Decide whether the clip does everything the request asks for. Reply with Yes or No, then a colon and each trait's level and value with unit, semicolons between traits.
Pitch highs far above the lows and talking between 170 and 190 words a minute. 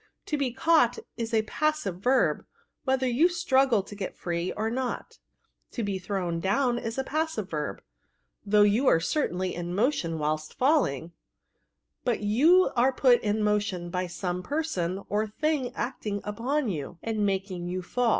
No: wide, 6.1 semitones; average, 160 wpm